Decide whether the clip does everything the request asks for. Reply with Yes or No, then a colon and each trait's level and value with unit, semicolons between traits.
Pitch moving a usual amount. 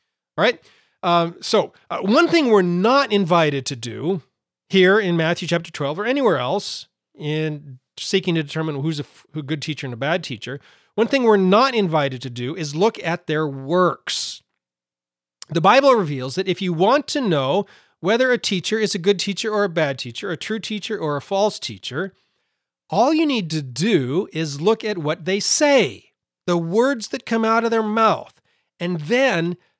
No: wide, 5.7 semitones